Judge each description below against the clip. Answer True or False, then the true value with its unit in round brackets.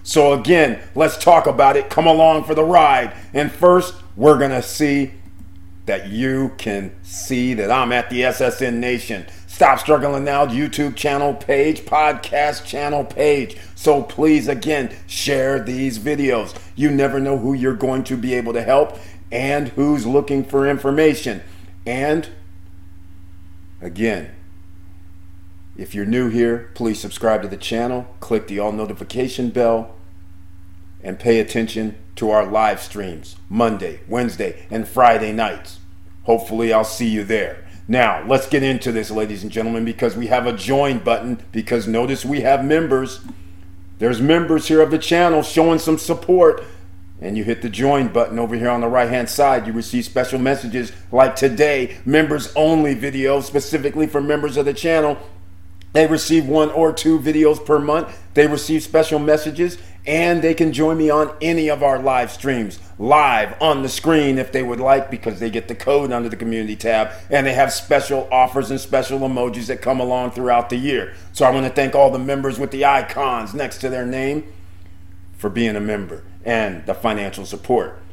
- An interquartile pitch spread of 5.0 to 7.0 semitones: True (5.4 semitones)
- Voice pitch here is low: True (125 Hz)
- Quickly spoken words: False (170 wpm)